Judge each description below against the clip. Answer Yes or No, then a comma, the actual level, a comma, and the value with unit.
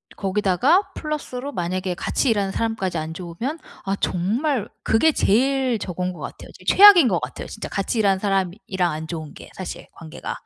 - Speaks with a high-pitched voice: Yes, high, 195 Hz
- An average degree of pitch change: No, wide, 5.9 semitones